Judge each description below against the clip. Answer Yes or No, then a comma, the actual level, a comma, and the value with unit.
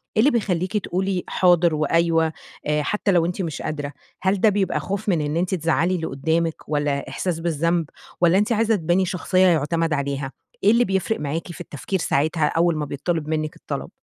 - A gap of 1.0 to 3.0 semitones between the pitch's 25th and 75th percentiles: No, average, 3.4 semitones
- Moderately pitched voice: Yes, medium, 170 Hz